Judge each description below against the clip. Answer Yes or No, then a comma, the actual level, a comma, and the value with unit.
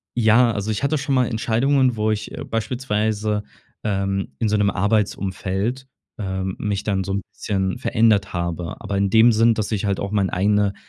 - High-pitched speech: No, low, 105 Hz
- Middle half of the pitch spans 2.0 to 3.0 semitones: Yes, narrow, 2.4 semitones